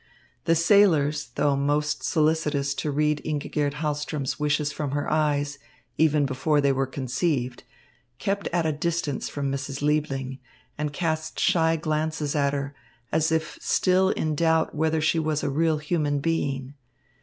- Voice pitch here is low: No, medium, 150 Hz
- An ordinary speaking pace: Yes, average, 150 wpm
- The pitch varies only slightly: Yes, narrow, 2.1 semitones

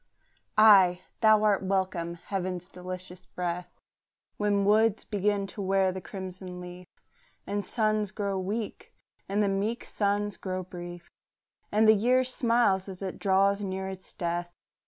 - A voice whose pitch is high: Yes, high, 195 Hz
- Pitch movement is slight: Yes, narrow, 2.2 semitones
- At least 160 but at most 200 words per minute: No, average, 140 wpm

